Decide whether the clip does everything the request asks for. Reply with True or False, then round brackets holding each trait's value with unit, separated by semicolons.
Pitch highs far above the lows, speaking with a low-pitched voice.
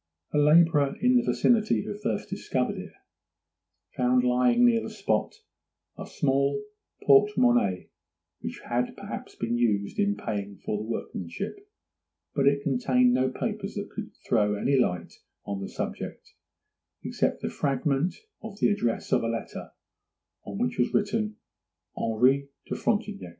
True (8.2 semitones; 130 Hz)